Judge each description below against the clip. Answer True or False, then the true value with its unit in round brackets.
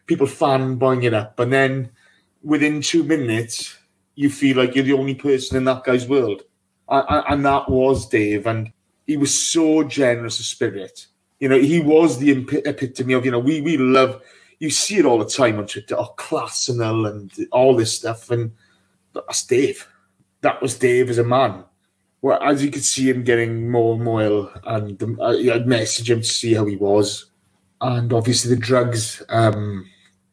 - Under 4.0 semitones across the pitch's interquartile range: True (3.4 semitones)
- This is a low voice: True (125 Hz)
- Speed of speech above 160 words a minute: True (190 wpm)